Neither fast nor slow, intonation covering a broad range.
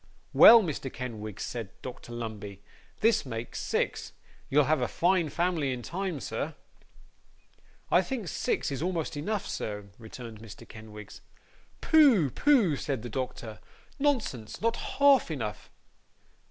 No: slow, 130 wpm; wide, 8.7 semitones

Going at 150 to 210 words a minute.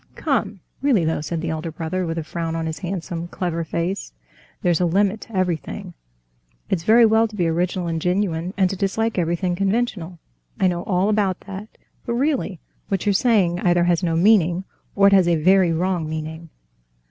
Yes: average, 185 wpm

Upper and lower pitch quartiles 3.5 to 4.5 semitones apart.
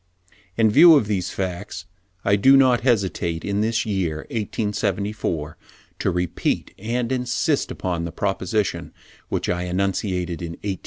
Yes: average, 4.2 semitones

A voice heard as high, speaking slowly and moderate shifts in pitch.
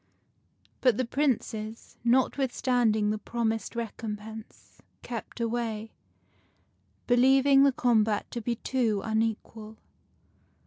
No: high, 230 Hz; slow, 95 wpm; narrow, 2.3 semitones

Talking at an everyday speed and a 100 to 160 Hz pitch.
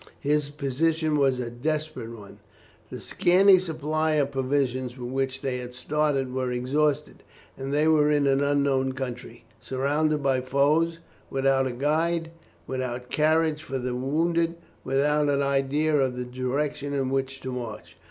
Yes: average, 150 wpm; medium, 140 Hz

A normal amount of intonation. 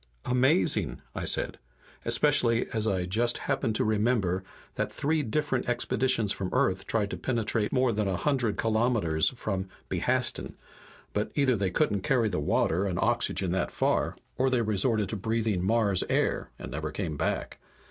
Yes: average, 4.2 semitones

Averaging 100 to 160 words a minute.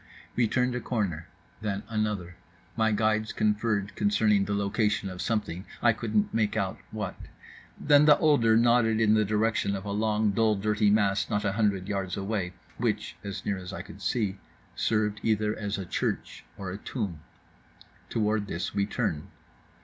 No: average, 170 wpm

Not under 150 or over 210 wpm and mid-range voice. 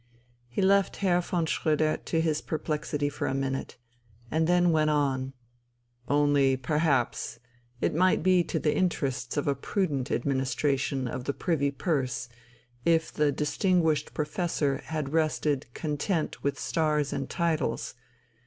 No: slow, 135 wpm; medium, 150 Hz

